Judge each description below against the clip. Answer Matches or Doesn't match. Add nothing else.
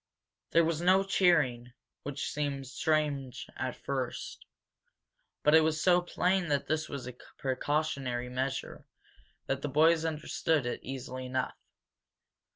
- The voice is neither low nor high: Matches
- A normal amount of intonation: Matches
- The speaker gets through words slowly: Matches